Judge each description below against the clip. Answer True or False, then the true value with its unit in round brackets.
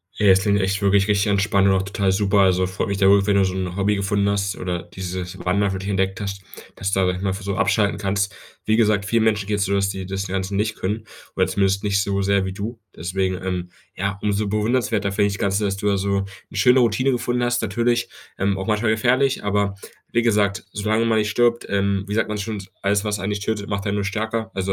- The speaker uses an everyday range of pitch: False (1.5 semitones)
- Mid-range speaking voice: False (100 Hz)